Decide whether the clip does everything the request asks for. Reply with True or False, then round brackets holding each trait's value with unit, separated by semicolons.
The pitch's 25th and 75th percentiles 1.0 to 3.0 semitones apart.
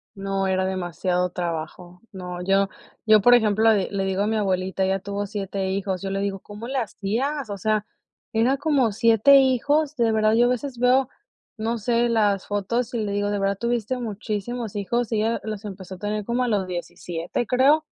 False (3.6 semitones)